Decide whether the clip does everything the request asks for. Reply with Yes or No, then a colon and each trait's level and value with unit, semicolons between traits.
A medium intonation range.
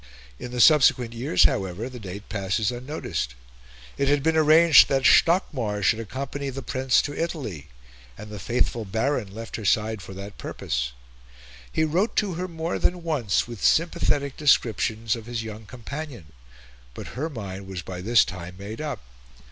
No: wide, 6.1 semitones